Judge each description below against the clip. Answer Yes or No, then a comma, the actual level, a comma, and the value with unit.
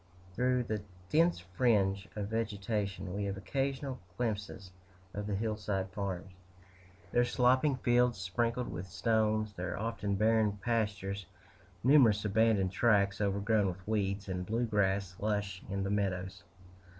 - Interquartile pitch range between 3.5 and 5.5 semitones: No, average, 2.8 semitones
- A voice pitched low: Yes, low, 105 Hz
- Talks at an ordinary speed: No, slow, 130 wpm